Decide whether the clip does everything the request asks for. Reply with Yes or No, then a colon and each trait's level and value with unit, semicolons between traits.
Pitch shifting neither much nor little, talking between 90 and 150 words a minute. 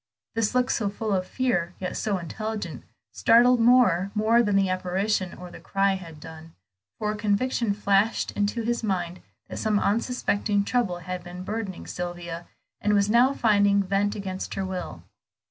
No: average, 3.2 semitones; average, 165 wpm